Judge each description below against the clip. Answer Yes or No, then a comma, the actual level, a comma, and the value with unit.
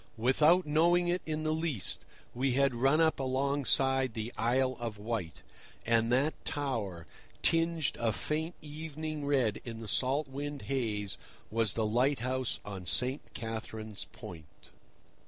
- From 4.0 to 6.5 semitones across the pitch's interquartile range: Yes, average, 4.8 semitones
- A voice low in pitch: Yes, low, 130 Hz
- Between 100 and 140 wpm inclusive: Yes, slow, 135 wpm